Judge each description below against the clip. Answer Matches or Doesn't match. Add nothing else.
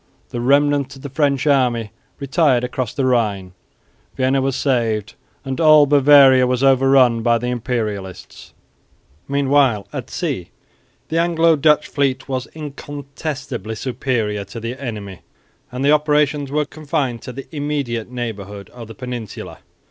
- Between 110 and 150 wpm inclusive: Matches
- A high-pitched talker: Doesn't match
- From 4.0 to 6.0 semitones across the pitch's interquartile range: Doesn't match